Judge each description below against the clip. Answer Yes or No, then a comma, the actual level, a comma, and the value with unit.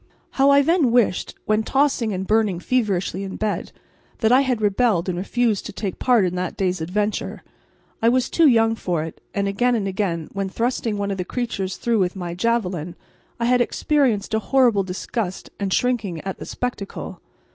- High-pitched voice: Yes, high, 210 Hz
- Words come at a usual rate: Yes, average, 190 wpm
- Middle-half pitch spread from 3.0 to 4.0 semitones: No, average, 4.4 semitones